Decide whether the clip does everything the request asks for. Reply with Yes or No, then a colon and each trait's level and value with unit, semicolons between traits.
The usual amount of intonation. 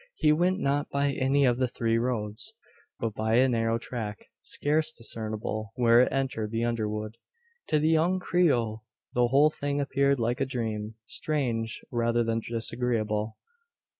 Yes: average, 3.7 semitones